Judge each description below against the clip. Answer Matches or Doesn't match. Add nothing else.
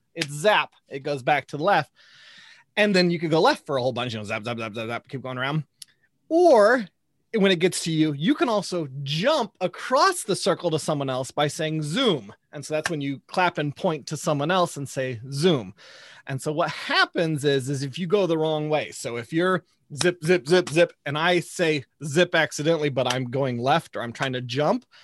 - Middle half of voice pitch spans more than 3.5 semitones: Matches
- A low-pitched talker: Doesn't match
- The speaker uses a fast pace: Matches